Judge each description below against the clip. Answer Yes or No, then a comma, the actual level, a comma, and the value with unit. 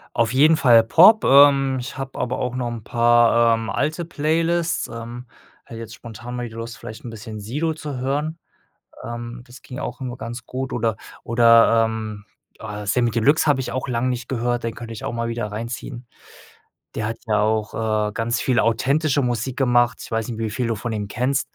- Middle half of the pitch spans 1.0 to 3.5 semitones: Yes, narrow, 2.5 semitones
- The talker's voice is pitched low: Yes, low, 120 Hz